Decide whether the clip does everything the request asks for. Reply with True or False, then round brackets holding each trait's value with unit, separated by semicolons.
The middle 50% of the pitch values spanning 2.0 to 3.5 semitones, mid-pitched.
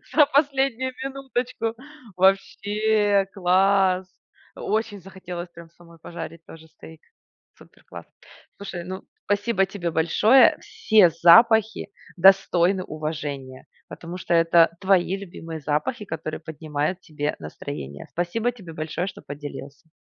False (4.1 semitones; 180 Hz)